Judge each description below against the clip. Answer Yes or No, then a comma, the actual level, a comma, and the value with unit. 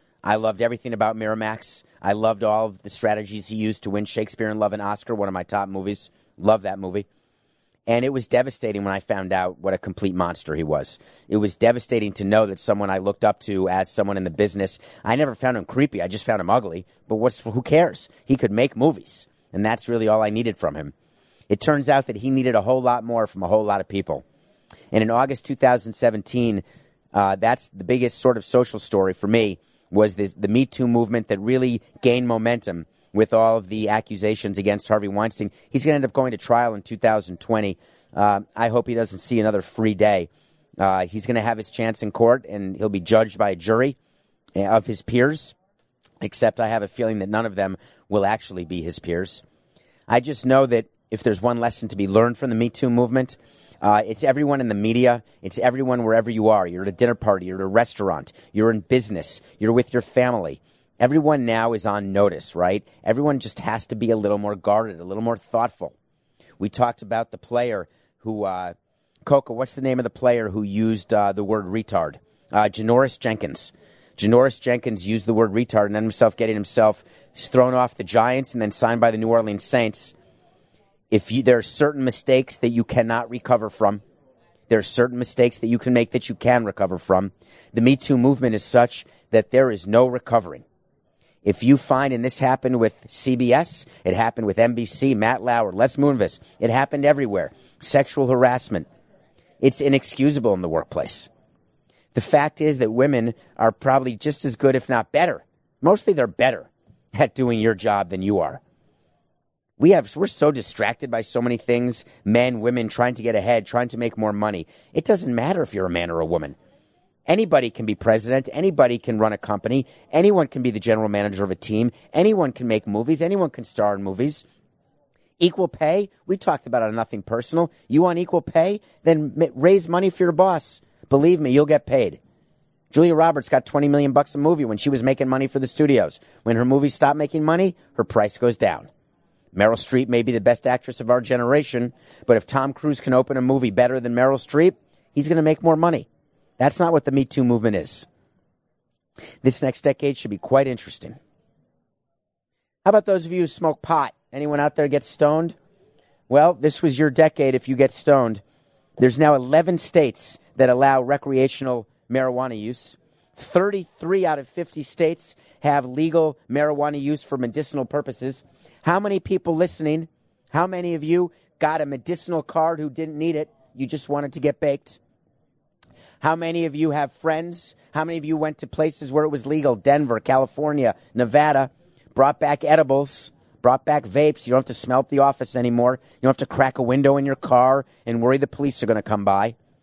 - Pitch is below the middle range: Yes, low, 120 Hz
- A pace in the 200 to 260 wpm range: Yes, fast, 205 wpm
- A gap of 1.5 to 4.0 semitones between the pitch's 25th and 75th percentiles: No, average, 4.5 semitones